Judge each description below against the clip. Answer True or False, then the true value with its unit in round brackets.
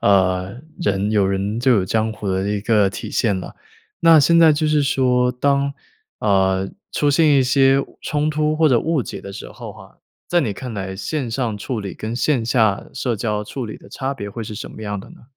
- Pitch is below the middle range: True (115 Hz)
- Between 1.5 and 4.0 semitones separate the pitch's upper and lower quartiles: False (5.5 semitones)